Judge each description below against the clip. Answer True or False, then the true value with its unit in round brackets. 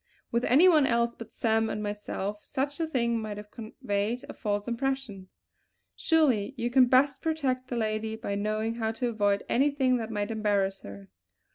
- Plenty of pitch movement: False (3.7 semitones)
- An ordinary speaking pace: True (175 wpm)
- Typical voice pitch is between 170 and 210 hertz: False (225 Hz)